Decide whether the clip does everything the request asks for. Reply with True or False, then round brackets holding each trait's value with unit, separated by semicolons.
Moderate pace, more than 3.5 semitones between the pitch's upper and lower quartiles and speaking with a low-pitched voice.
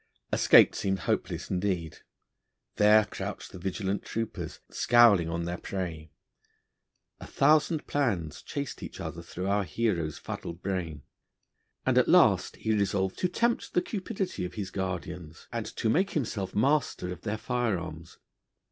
True (145 wpm; 4.9 semitones; 95 Hz)